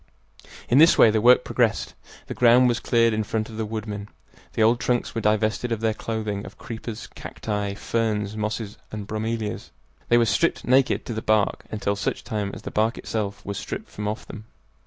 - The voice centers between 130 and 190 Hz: No, low, 110 Hz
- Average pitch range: No, narrow, 1.7 semitones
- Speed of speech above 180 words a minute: Yes, average, 200 wpm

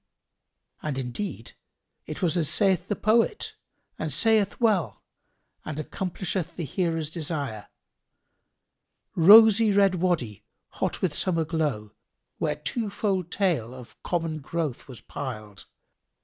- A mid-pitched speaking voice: Yes, medium, 165 Hz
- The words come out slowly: Yes, slow, 120 wpm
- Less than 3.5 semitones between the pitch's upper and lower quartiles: No, average, 5.1 semitones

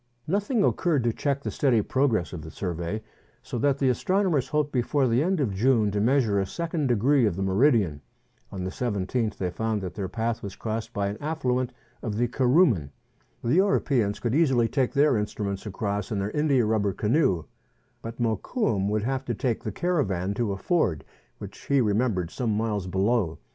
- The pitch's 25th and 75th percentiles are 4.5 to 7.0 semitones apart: Yes, wide, 5.4 semitones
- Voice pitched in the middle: No, low, 115 Hz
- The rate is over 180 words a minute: Yes, average, 190 wpm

